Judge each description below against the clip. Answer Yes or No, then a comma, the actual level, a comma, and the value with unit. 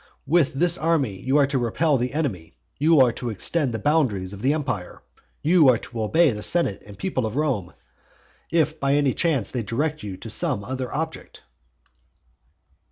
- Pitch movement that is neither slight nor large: No, wide, 5.8 semitones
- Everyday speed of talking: Yes, average, 180 wpm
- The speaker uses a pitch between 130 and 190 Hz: Yes, low, 135 Hz